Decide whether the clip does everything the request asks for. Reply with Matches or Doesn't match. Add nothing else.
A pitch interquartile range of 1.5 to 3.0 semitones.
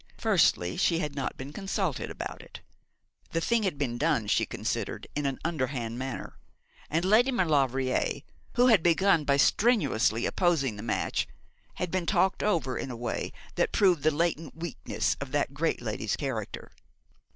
Doesn't match